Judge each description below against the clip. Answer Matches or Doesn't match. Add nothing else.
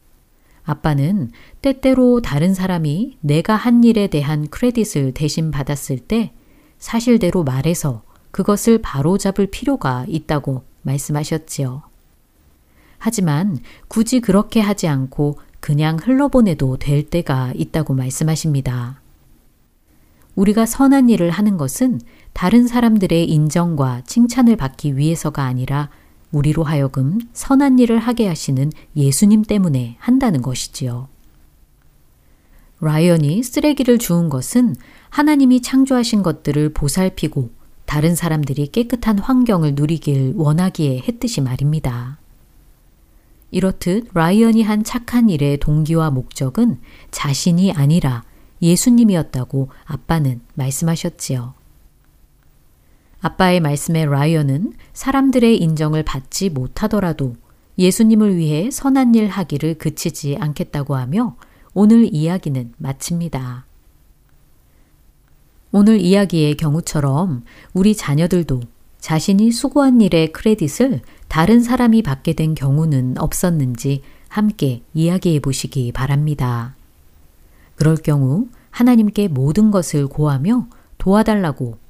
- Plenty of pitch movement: Matches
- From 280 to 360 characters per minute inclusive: Doesn't match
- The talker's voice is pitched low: Doesn't match